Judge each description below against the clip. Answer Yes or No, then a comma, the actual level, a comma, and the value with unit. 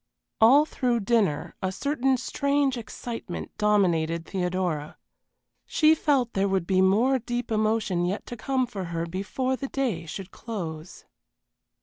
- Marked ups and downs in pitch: Yes, wide, 5.7 semitones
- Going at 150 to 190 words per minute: No, slow, 135 wpm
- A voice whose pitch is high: Yes, high, 215 Hz